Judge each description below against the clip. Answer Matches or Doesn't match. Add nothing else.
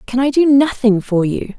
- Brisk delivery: Matches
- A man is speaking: Doesn't match